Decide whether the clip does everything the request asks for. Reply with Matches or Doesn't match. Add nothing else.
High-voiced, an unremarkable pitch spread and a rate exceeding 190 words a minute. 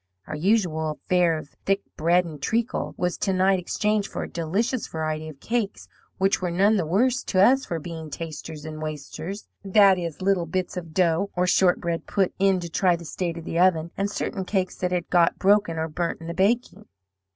Doesn't match